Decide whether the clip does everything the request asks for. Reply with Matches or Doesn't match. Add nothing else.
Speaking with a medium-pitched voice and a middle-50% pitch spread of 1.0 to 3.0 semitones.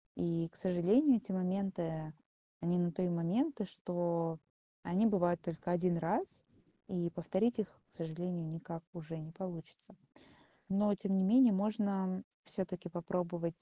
Matches